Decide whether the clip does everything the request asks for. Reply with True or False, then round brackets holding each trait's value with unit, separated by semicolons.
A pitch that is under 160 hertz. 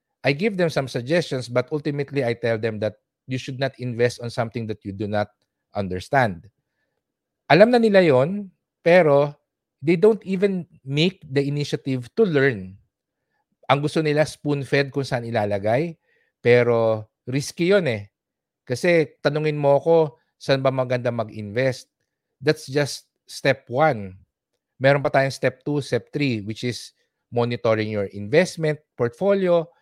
True (135 Hz)